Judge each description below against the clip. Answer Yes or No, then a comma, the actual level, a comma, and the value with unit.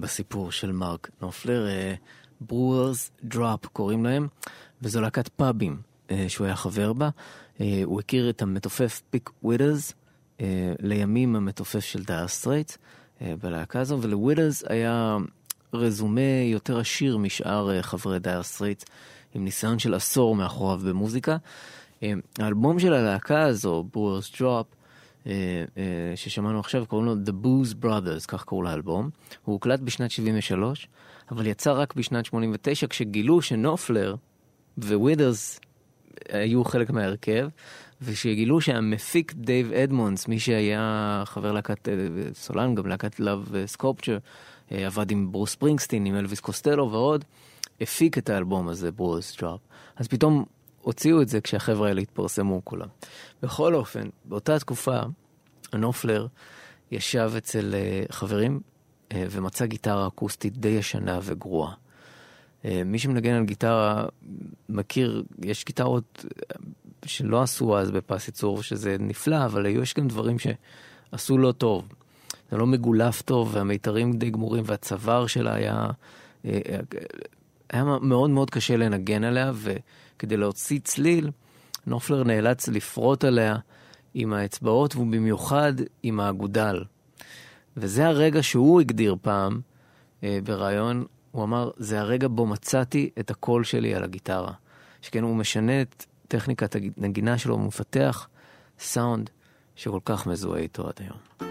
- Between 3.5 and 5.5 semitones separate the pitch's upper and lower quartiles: Yes, average, 4.0 semitones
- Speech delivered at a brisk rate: No, average, 130 wpm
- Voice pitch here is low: Yes, low, 115 Hz